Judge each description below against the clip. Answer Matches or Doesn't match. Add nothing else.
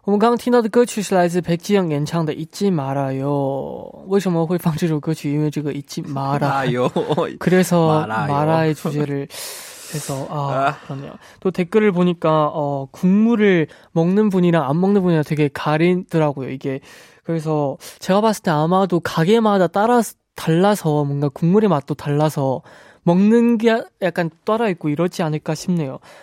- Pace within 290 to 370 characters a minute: Matches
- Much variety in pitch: Doesn't match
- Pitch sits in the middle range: Matches